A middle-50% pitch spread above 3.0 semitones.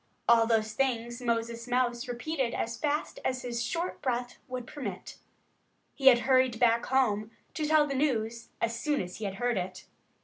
No: narrow, 2.4 semitones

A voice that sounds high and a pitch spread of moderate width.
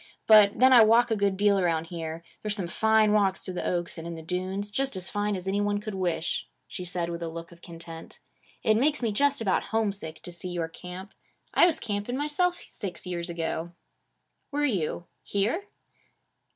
Yes: high, 195 Hz; average, 4.2 semitones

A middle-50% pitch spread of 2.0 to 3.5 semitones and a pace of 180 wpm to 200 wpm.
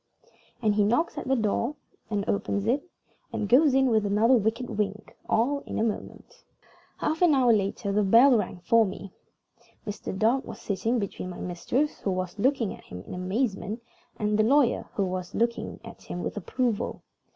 No: average, 4.0 semitones; average, 185 wpm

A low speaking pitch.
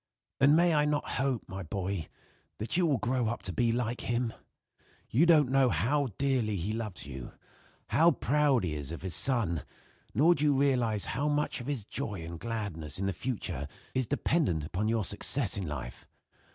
Yes: low, 115 Hz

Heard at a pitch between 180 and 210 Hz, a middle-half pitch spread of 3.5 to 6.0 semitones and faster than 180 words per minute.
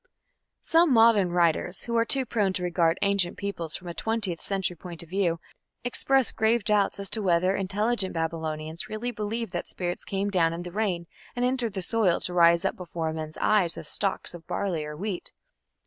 Yes: high, 190 Hz; average, 4.1 semitones; average, 195 wpm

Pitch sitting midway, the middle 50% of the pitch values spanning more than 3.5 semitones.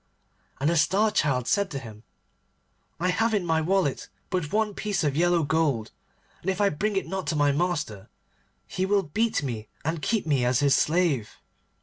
Yes: medium, 165 Hz; average, 5.2 semitones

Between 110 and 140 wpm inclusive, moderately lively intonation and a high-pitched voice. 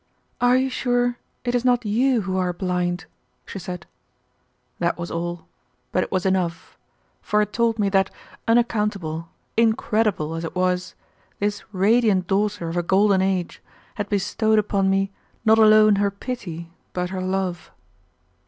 No: average, 155 wpm; average, 3.3 semitones; high, 195 Hz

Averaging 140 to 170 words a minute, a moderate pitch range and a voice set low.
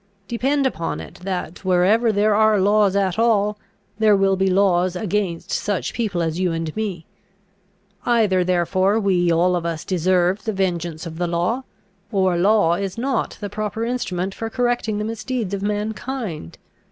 No: average, 165 wpm; average, 3.4 semitones; high, 195 Hz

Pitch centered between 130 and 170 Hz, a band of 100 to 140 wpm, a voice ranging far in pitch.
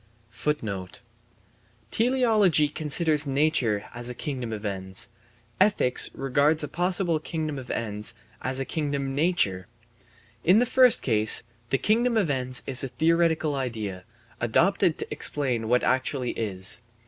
Yes: medium, 140 Hz; slow, 135 wpm; wide, 5.7 semitones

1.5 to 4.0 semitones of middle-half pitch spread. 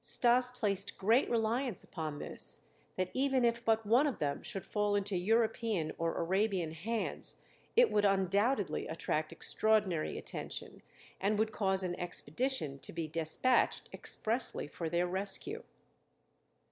No: average, 4.8 semitones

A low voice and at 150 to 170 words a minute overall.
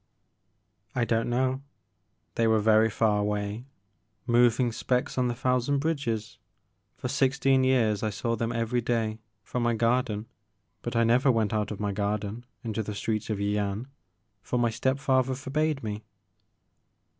Yes: low, 115 Hz; average, 160 wpm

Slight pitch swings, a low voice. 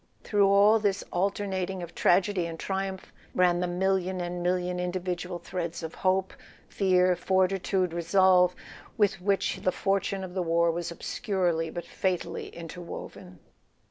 No: narrow, 1.6 semitones; medium, 180 Hz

